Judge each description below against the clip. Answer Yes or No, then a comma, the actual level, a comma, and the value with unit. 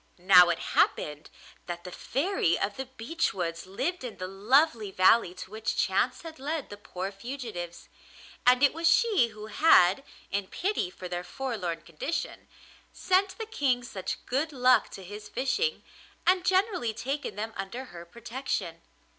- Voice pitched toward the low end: No, high, 230 Hz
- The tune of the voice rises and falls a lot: Yes, wide, 7.4 semitones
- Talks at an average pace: Yes, average, 160 wpm